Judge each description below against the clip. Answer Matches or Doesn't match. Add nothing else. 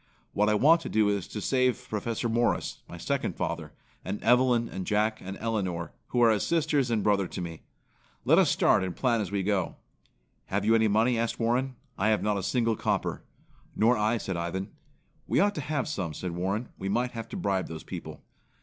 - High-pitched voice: Doesn't match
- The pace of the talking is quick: Matches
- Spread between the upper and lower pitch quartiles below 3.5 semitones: Doesn't match